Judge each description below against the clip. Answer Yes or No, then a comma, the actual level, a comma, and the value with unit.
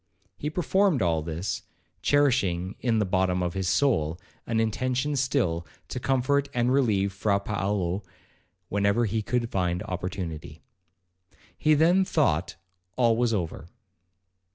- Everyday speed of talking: No, slow, 130 wpm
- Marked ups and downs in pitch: Yes, wide, 6.0 semitones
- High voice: No, low, 105 Hz